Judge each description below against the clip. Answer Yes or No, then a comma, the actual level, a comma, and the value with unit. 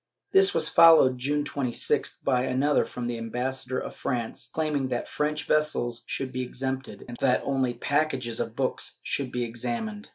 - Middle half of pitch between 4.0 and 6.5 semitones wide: No, average, 3.2 semitones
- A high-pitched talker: No, low, 130 Hz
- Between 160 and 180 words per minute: Yes, average, 170 wpm